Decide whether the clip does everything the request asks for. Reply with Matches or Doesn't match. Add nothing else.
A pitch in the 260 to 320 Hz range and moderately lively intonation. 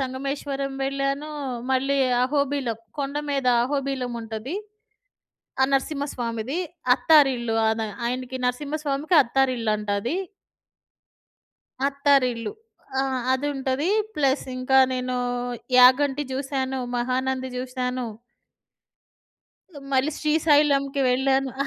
Doesn't match